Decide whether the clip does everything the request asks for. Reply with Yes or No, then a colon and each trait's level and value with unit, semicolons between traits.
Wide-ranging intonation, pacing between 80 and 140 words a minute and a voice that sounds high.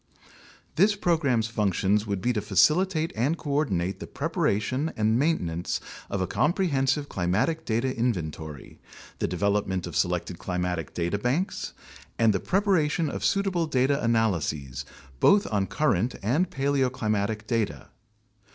No: wide, 7.9 semitones; slow, 135 wpm; low, 115 Hz